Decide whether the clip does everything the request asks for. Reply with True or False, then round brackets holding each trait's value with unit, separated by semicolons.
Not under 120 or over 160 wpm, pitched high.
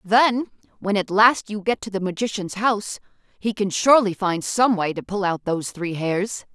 False (200 wpm; 200 Hz)